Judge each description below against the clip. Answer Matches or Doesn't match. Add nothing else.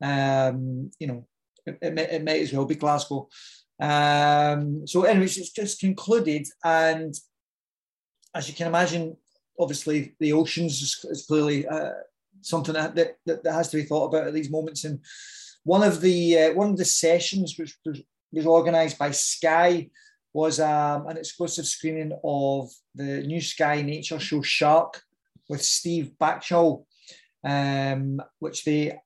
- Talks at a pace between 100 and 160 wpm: Matches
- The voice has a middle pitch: Matches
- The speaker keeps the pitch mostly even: Matches